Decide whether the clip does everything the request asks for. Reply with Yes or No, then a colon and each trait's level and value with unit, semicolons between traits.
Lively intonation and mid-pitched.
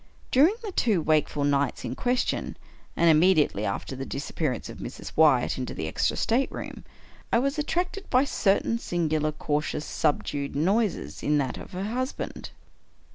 Yes: wide, 8.7 semitones; medium, 160 Hz